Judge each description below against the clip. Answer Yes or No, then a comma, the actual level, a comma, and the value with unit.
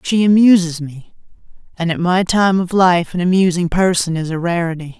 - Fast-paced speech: No, average, 180 wpm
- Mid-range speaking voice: Yes, medium, 175 Hz